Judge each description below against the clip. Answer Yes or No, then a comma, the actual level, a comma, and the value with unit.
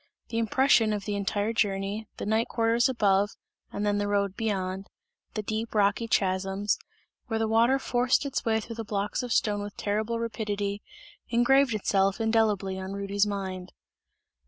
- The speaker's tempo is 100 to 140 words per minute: No, average, 160 wpm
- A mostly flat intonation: Yes, narrow, 2.2 semitones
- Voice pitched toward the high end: Yes, high, 210 Hz